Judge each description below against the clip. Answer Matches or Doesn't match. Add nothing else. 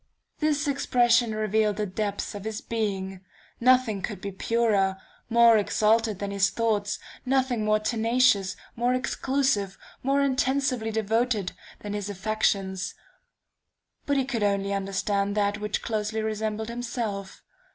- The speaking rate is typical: Doesn't match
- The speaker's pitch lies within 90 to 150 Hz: Doesn't match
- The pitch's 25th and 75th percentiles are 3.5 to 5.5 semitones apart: Doesn't match